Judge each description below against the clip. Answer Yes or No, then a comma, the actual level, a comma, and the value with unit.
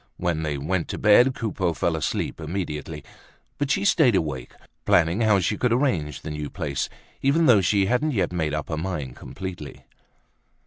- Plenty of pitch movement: Yes, wide, 6.2 semitones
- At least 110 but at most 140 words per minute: No, average, 175 wpm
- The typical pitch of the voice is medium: No, very low, 90 Hz